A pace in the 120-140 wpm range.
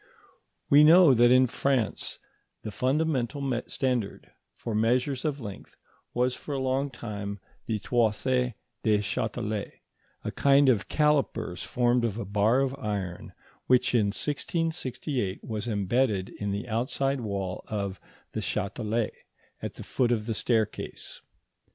Yes: slow, 135 wpm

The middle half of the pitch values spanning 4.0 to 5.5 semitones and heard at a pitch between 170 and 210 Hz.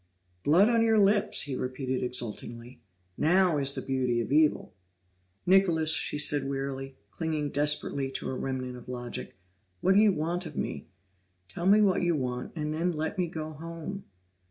No: average, 5.0 semitones; medium, 150 Hz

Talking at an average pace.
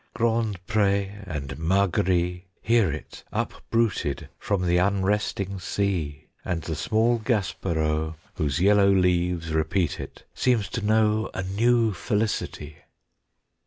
No: slow, 115 wpm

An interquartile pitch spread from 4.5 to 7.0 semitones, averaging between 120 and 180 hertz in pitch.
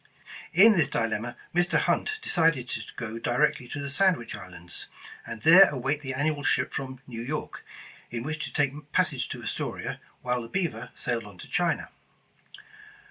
Yes: average, 5.1 semitones; low, 135 Hz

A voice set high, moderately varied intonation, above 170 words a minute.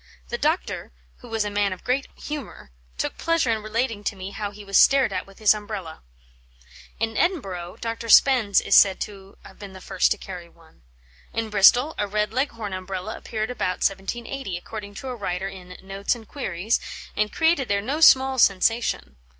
Yes: high, 210 Hz; average, 3.7 semitones; average, 185 wpm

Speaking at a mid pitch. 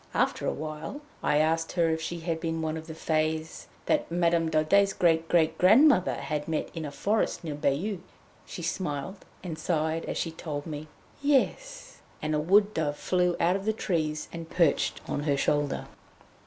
Yes: medium, 165 Hz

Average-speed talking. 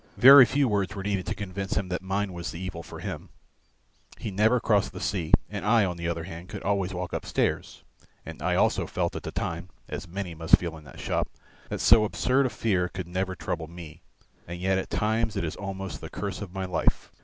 No: fast, 225 wpm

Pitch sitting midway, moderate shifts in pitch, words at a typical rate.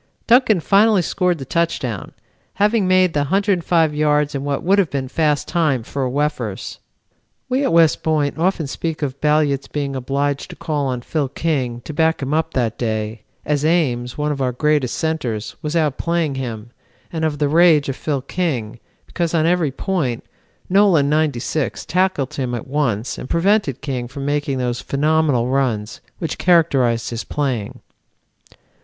Yes: medium, 150 Hz; average, 4.1 semitones; average, 165 wpm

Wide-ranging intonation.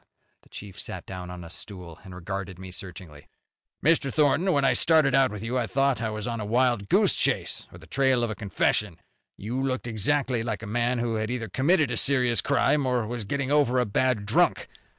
No: average, 4.8 semitones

